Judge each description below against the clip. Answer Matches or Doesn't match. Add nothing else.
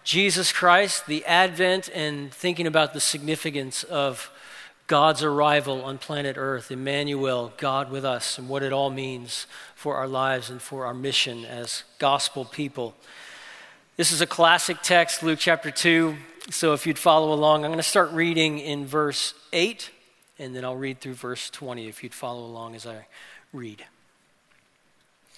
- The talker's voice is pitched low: Doesn't match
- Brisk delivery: Doesn't match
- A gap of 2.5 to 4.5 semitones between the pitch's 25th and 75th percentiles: Matches